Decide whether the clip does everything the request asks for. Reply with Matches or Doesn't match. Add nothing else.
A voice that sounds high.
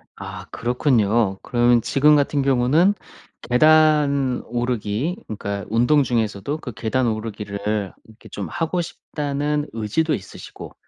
Doesn't match